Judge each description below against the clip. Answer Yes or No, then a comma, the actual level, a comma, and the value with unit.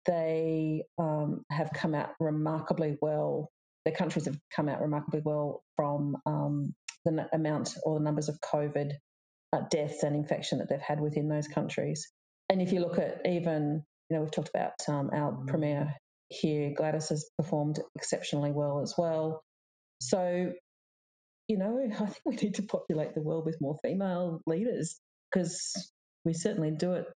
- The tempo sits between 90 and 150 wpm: No, average, 170 wpm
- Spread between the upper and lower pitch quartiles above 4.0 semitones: No, narrow, 2.5 semitones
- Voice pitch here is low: No, medium, 155 Hz